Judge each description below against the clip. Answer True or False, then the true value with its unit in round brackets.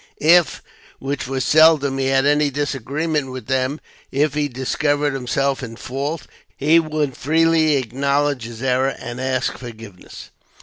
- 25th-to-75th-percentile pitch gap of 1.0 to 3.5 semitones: True (2.4 semitones)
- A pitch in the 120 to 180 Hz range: True (140 Hz)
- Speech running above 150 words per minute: False (140 wpm)